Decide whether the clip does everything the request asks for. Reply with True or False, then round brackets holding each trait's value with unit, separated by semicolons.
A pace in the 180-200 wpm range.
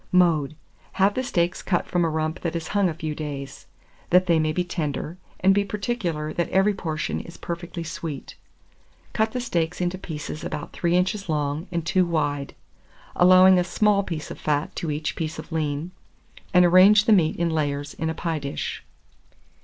True (185 wpm)